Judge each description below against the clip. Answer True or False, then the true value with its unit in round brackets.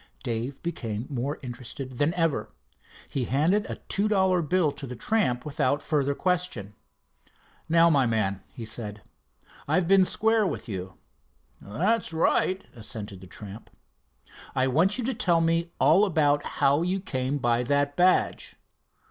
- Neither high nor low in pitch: True (145 Hz)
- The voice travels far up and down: True (6.9 semitones)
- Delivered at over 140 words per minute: True (150 wpm)